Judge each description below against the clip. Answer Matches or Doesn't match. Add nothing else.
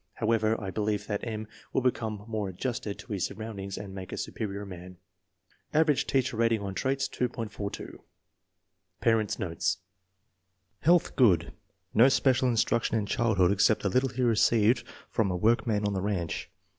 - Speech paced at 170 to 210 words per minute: Doesn't match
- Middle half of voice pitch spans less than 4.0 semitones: Matches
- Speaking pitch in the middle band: Doesn't match